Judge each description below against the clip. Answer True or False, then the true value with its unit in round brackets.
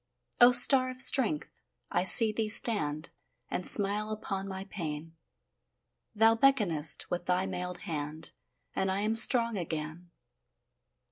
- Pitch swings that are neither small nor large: True (4.8 semitones)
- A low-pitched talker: False (195 Hz)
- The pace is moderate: False (130 wpm)